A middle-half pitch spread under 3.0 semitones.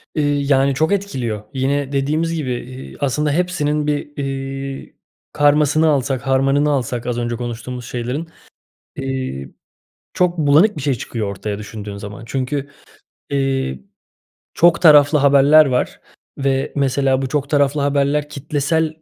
Yes: narrow, 2.5 semitones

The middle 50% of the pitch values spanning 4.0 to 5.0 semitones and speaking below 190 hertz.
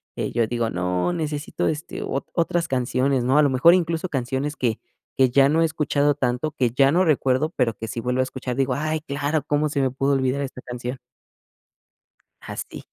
No: average, 3.2 semitones; low, 135 Hz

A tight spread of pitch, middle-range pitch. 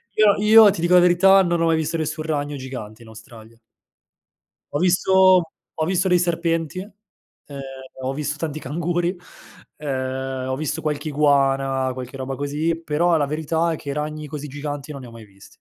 No: average, 4.1 semitones; medium, 150 Hz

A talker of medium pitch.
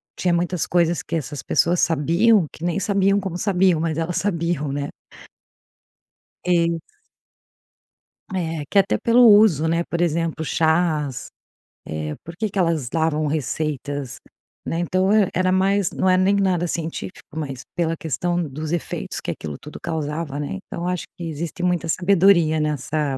Yes: medium, 170 Hz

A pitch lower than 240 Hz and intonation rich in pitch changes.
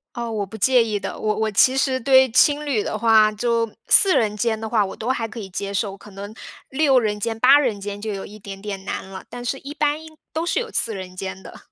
No: high, 220 Hz; average, 4.2 semitones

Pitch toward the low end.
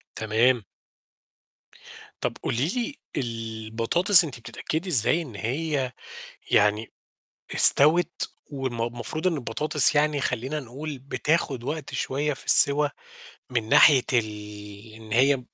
Yes: low, 130 Hz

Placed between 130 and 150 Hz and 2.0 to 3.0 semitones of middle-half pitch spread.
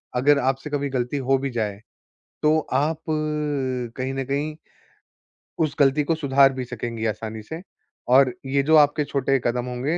Yes: low, 135 Hz; narrow, 2.6 semitones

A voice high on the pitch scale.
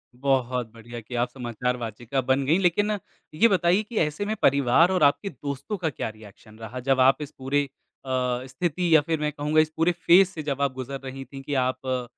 No: low, 135 Hz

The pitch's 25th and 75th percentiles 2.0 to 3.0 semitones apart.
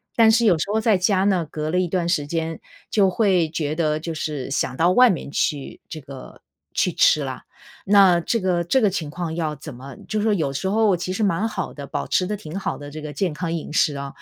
No: average, 4.3 semitones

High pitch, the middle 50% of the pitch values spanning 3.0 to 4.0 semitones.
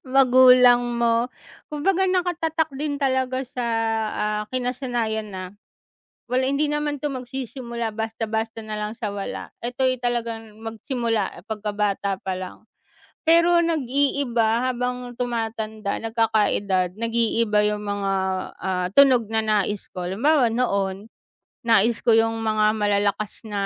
Yes: high, 230 Hz; average, 3.3 semitones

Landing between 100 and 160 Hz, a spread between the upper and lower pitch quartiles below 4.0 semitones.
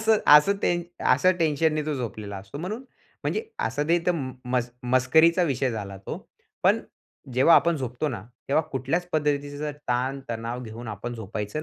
No: low, 135 Hz; average, 4.8 semitones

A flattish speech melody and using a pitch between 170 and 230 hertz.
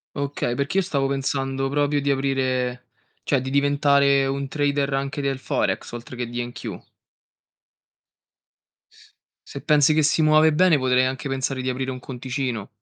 No: narrow, 1.6 semitones; low, 135 Hz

